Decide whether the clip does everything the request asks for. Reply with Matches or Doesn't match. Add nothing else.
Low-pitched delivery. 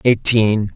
Matches